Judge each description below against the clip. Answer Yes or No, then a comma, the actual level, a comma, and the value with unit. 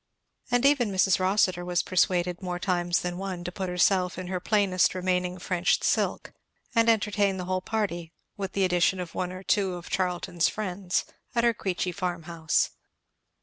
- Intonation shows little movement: Yes, narrow, 1.7 semitones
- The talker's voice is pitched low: No, medium, 185 Hz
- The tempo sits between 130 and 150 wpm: No, average, 175 wpm